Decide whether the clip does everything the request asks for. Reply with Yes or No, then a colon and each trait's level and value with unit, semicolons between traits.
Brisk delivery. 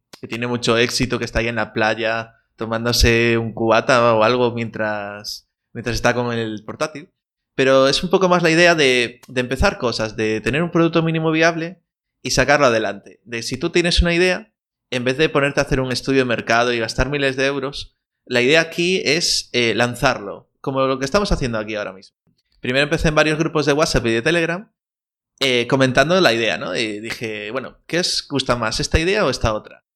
Yes: fast, 205 wpm